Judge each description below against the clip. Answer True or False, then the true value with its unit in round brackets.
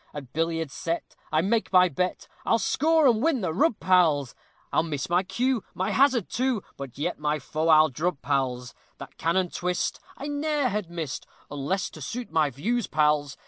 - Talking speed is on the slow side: False (185 wpm)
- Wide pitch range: True (7.3 semitones)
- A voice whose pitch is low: False (175 Hz)